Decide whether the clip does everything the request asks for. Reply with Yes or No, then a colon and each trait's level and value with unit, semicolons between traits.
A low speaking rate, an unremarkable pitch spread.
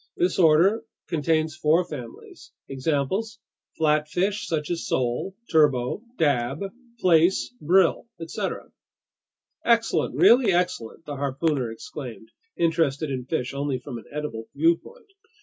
Yes: slow, 115 wpm; average, 4.4 semitones